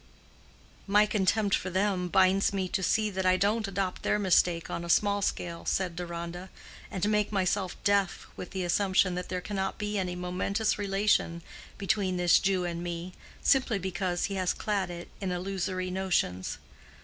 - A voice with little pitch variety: Yes, narrow, 2.1 semitones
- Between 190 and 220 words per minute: No, average, 170 wpm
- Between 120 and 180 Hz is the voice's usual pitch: No, high, 190 Hz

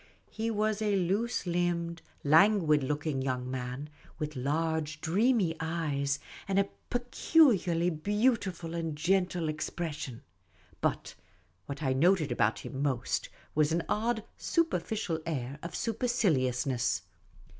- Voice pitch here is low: No, medium, 165 Hz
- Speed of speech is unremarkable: No, slow, 115 wpm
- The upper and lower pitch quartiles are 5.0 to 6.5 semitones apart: Yes, wide, 5.5 semitones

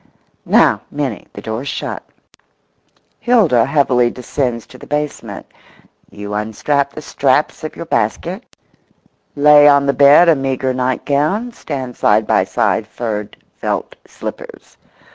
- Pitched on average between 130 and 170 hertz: Yes, medium, 140 Hz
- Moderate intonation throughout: Yes, average, 3.8 semitones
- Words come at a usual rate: No, slow, 125 wpm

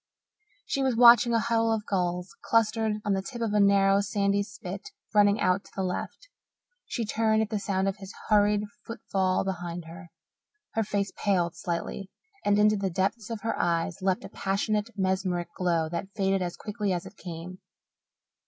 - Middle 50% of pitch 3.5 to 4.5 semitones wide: No, narrow, 2.4 semitones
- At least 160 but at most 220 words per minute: Yes, average, 180 wpm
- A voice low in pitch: No, high, 200 Hz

